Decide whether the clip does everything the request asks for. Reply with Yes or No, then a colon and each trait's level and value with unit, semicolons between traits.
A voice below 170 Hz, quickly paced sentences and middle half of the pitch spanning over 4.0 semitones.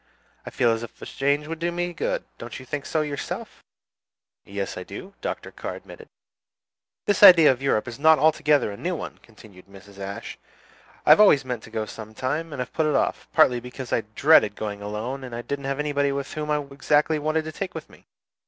Yes: medium, 140 Hz; fast, 210 wpm; average, 5.2 semitones